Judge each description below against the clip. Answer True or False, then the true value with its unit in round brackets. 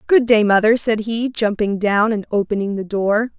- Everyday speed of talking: True (195 wpm)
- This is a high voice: True (215 Hz)